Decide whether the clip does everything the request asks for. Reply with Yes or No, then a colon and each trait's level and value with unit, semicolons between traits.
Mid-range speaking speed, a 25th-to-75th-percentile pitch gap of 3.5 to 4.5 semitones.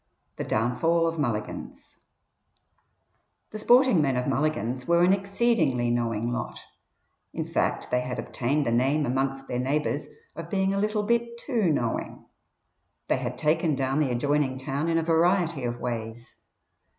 No: average, 150 wpm; wide, 5.5 semitones